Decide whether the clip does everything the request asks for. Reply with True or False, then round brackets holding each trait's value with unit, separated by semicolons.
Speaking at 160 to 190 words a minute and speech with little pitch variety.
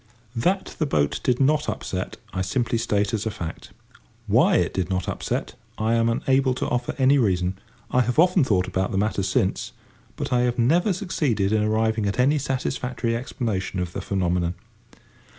False (180 wpm; 5.3 semitones)